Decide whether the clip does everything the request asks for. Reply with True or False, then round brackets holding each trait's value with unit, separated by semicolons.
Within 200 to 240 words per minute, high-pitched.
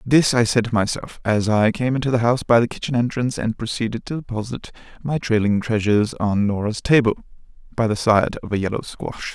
False (205 wpm; 115 Hz)